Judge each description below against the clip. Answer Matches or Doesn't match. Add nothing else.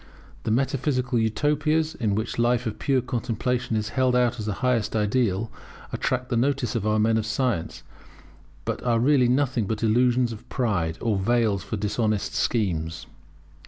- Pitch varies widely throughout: Doesn't match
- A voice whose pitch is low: Matches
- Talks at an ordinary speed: Matches